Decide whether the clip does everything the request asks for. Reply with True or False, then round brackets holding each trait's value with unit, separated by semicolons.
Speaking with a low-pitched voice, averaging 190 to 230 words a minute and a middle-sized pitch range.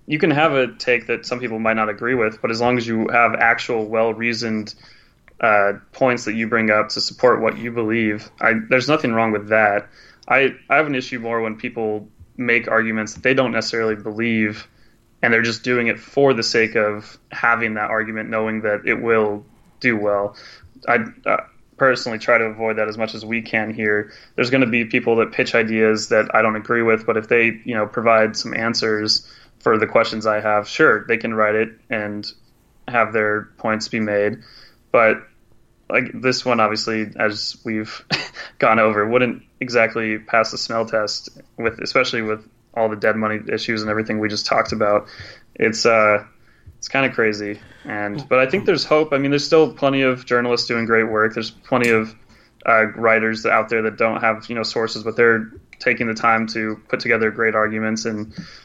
False (110 Hz; 200 wpm; 1.4 semitones)